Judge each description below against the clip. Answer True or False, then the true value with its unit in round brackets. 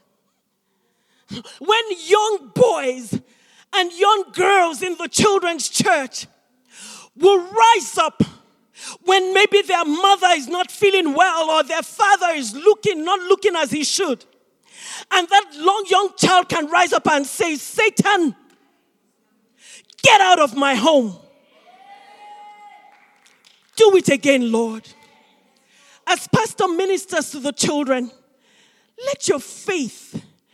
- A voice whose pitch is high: True (335 Hz)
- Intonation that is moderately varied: False (6.8 semitones)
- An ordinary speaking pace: False (120 wpm)